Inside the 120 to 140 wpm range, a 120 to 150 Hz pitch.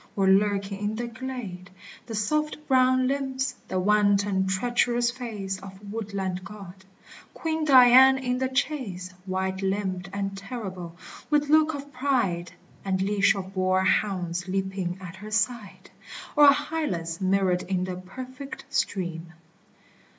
No: slow, 135 wpm; high, 200 Hz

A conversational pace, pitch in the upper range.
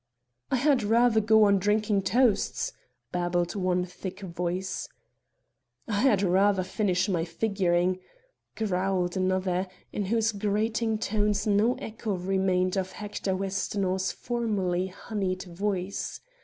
No: slow, 115 wpm; high, 195 Hz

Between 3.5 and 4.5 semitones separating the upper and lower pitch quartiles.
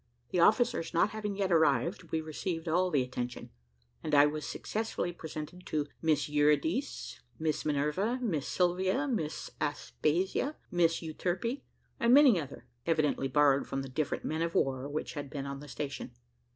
Yes: average, 4.1 semitones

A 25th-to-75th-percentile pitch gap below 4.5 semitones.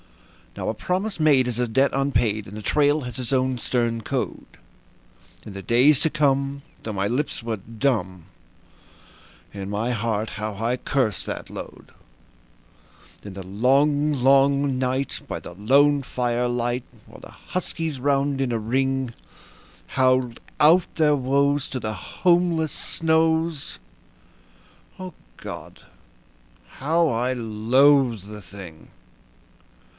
Yes: average, 4.1 semitones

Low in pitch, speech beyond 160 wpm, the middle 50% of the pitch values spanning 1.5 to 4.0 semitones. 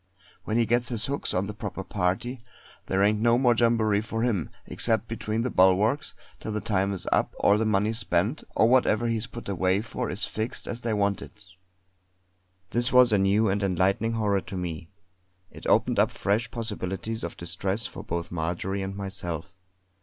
Yes: low, 105 Hz; average, 190 wpm; average, 3.1 semitones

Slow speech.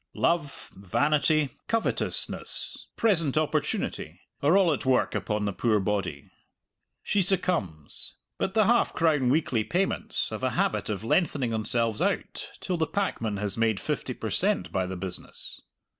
No: average, 145 wpm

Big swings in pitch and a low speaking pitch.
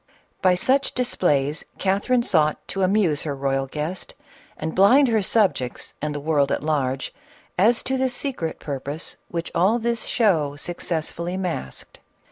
No: wide, 6.6 semitones; medium, 170 Hz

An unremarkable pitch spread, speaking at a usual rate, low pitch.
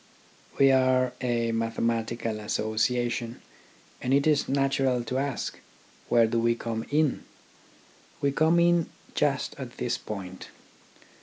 No: average, 3.1 semitones; slow, 125 wpm; low, 120 Hz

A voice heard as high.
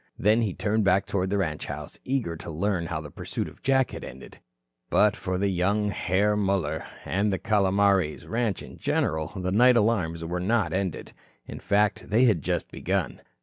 No: low, 100 Hz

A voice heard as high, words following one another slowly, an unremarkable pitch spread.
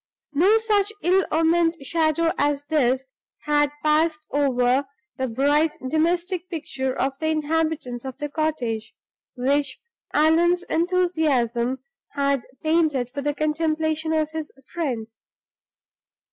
Yes: very high, 305 Hz; slow, 115 wpm; average, 3.1 semitones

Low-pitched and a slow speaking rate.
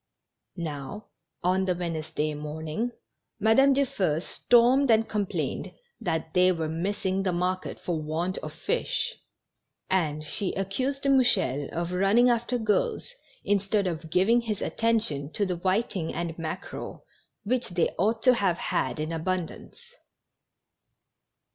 No: medium, 185 Hz; slow, 130 wpm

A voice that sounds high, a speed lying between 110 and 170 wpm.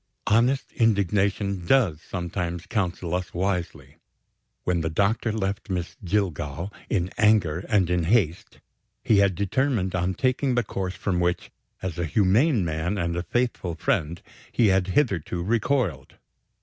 No: very low, 95 Hz; average, 140 wpm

